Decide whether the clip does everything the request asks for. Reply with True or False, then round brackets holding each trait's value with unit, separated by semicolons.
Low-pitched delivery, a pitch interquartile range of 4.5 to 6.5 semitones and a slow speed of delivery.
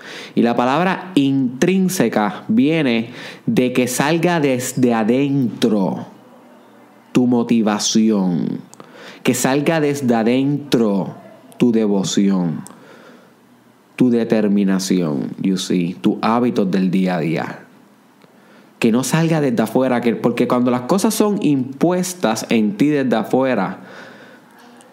True (125 Hz; 5.2 semitones; 105 wpm)